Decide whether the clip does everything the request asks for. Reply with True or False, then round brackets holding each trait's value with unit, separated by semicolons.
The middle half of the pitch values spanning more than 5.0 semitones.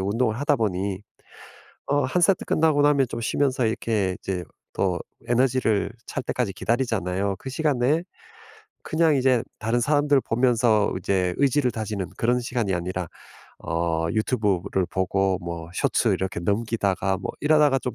True (5.6 semitones)